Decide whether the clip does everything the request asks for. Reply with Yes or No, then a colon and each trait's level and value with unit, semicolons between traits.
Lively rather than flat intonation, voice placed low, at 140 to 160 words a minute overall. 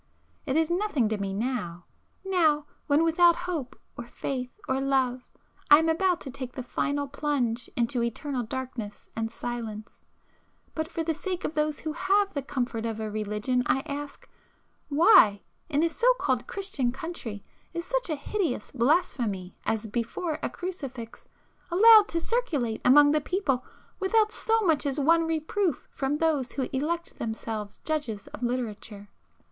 No: wide, 5.8 semitones; very high, 280 Hz; average, 155 wpm